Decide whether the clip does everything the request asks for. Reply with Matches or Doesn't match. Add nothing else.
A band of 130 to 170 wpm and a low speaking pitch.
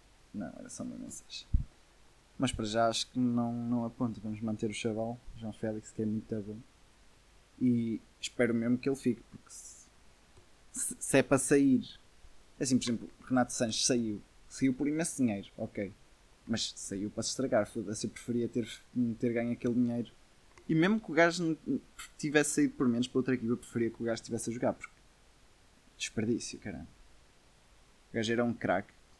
Doesn't match